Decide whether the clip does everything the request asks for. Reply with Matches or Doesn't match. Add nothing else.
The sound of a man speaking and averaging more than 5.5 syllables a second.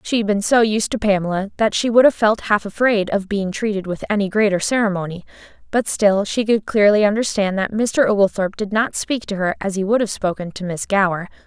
Doesn't match